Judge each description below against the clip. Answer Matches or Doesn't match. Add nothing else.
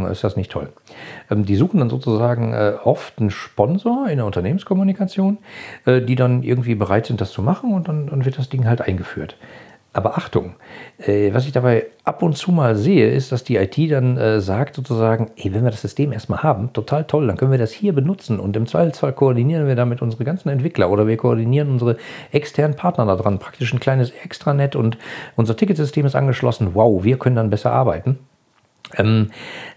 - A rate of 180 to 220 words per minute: Matches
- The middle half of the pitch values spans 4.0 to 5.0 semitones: Matches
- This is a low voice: Matches